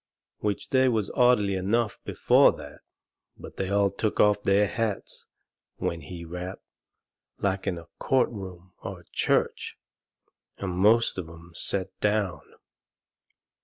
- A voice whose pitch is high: No, low, 100 Hz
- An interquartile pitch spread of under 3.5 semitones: Yes, narrow, 2.6 semitones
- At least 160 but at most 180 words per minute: No, slow, 135 wpm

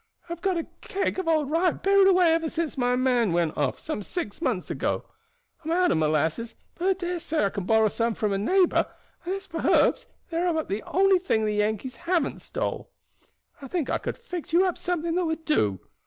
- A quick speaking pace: Yes, fast, 225 wpm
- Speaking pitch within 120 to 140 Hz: No, very high, 320 Hz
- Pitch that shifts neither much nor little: No, wide, 8.4 semitones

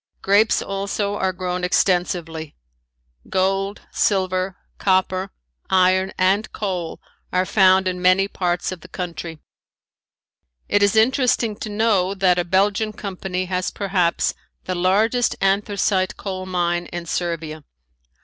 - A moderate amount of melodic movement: No, narrow, 1.8 semitones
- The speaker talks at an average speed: No, slow, 120 wpm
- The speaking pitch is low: No, medium, 185 Hz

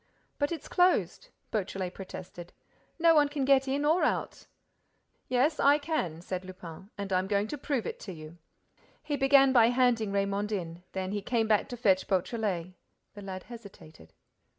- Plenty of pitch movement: Yes, wide, 6.5 semitones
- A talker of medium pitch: No, high, 210 Hz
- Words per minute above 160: Yes, average, 170 wpm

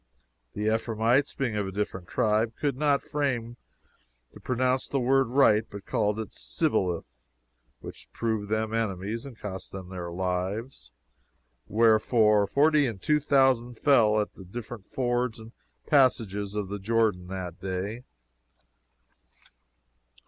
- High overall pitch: No, low, 110 Hz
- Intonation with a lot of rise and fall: No, average, 3.8 semitones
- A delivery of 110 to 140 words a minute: Yes, slow, 135 wpm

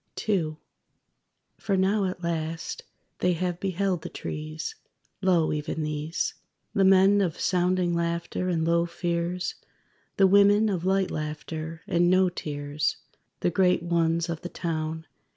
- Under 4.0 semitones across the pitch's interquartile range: Yes, narrow, 2.6 semitones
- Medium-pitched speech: Yes, medium, 170 Hz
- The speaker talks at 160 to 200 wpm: No, average, 140 wpm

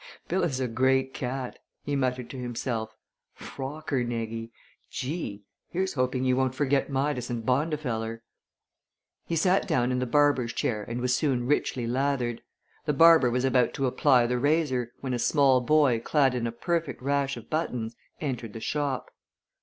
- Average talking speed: Yes, average, 160 wpm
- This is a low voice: Yes, low, 130 Hz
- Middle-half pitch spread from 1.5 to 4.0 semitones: Yes, average, 2.9 semitones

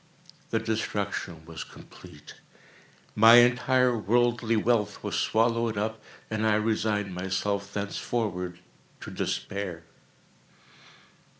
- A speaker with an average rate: No, slow, 95 wpm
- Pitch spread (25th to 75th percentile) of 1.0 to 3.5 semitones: Yes, average, 2.7 semitones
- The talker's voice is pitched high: No, low, 110 Hz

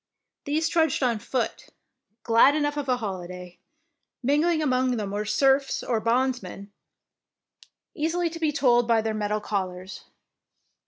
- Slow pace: Yes, slow, 130 wpm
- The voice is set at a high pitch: Yes, high, 245 Hz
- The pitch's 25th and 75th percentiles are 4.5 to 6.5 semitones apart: Yes, wide, 5.6 semitones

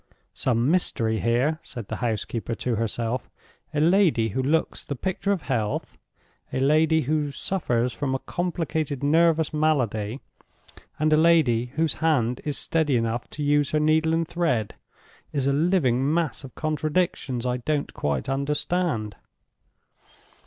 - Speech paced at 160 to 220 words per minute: No, average, 140 wpm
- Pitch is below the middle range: No, medium, 145 Hz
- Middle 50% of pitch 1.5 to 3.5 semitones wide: No, average, 4.8 semitones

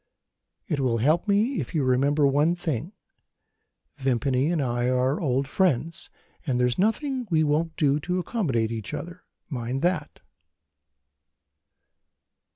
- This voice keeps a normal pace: No, slow, 130 wpm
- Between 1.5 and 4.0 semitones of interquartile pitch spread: No, average, 5.3 semitones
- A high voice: No, medium, 145 Hz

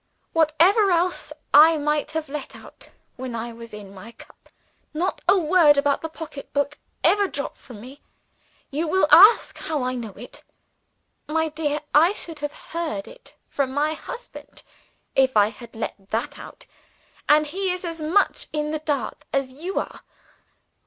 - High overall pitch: Yes, very high, 300 Hz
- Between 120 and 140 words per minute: No, average, 165 wpm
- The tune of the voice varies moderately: Yes, average, 3.9 semitones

